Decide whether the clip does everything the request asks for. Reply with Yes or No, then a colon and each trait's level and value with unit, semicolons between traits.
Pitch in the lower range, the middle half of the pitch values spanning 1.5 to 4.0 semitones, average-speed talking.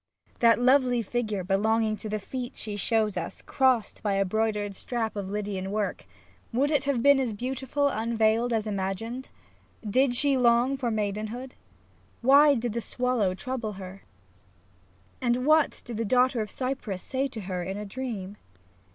No: high, 230 Hz; average, 3.7 semitones; average, 170 wpm